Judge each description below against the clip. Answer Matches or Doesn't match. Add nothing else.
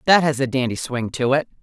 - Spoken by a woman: Matches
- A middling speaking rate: Doesn't match